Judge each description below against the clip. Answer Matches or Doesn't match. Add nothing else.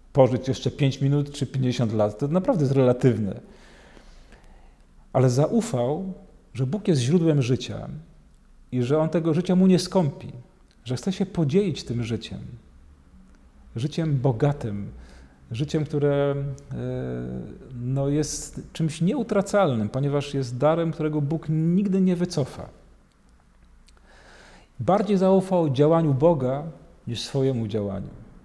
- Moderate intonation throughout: Doesn't match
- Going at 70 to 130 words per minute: Matches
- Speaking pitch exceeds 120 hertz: Matches